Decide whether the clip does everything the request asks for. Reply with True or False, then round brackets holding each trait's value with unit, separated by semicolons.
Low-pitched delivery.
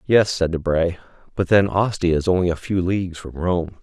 True (90 Hz)